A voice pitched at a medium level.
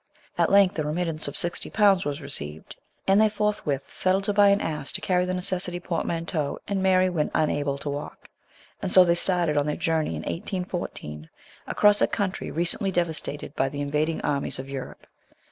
Yes: medium, 170 Hz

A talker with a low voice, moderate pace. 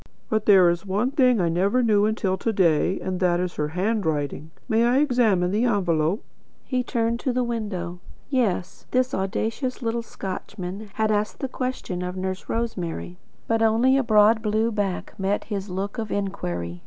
No: high, 205 Hz; average, 175 wpm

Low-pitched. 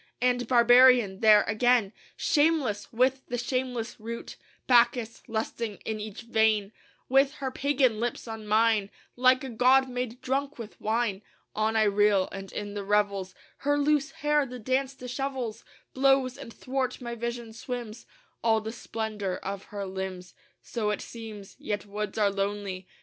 No: high, 230 Hz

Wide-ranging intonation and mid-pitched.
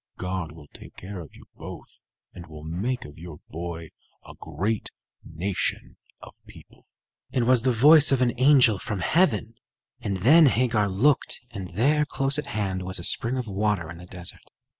No: wide, 6.6 semitones; low, 100 Hz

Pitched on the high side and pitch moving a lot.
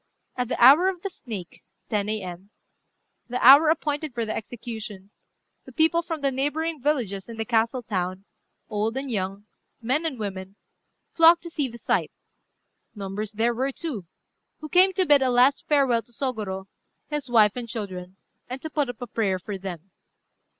Yes: high, 240 Hz; wide, 5.9 semitones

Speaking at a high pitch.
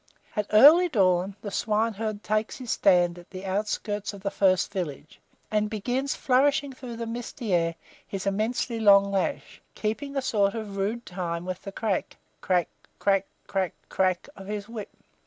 Yes: high, 205 Hz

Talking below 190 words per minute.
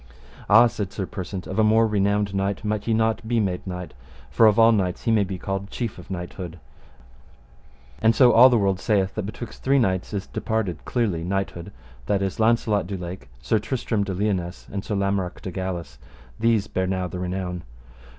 No: average, 195 wpm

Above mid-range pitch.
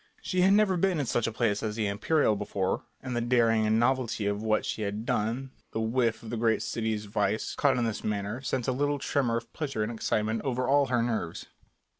No: low, 115 Hz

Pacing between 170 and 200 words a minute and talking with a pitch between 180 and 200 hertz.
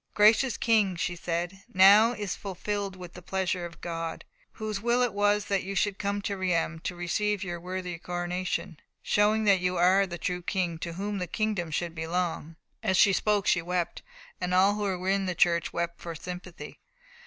Yes: average, 190 wpm; medium, 185 Hz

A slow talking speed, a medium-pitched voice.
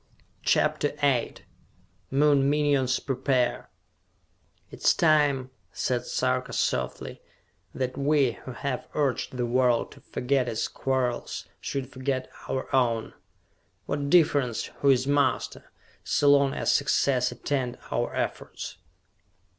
No: slow, 115 wpm; low, 130 Hz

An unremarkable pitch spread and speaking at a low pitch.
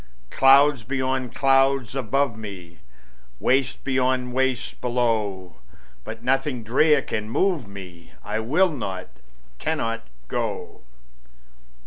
Yes: average, 3.7 semitones; low, 125 Hz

